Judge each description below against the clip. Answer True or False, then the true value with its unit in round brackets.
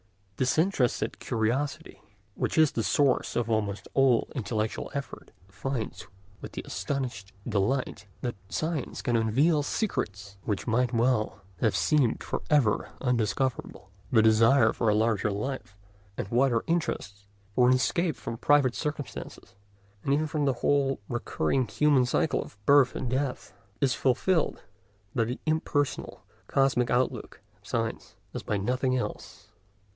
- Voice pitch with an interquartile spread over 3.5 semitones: True (3.9 semitones)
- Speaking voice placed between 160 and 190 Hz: False (125 Hz)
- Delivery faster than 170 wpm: False (135 wpm)